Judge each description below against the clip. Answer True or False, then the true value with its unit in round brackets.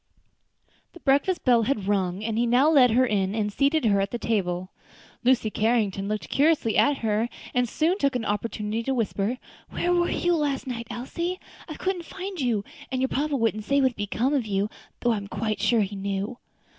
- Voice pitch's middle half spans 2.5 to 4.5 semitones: False (5.0 semitones)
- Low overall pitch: False (235 Hz)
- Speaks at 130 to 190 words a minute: False (205 wpm)